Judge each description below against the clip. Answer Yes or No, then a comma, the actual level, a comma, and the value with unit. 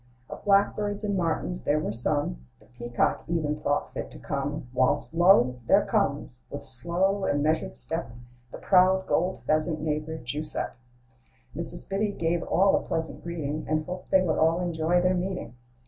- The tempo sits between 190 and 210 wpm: No, average, 170 wpm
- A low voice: No, medium, 160 Hz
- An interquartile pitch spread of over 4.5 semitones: No, average, 4.0 semitones